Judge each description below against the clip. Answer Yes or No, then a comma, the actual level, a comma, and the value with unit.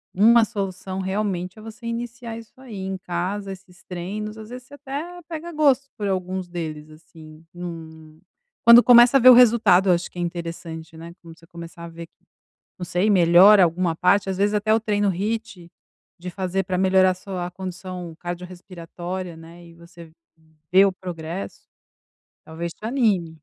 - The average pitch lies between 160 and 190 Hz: Yes, medium, 185 Hz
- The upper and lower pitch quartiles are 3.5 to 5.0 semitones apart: Yes, average, 3.8 semitones